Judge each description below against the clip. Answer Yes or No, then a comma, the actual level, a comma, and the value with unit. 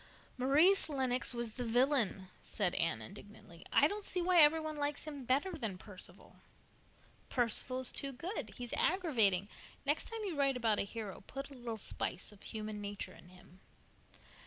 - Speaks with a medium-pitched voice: No, very high, 250 Hz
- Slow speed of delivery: No, average, 170 wpm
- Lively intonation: Yes, wide, 6.0 semitones